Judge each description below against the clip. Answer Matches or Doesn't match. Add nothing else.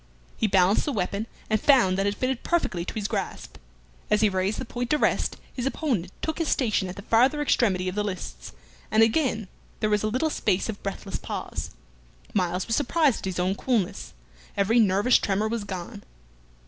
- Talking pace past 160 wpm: Matches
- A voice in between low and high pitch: Doesn't match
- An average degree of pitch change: Matches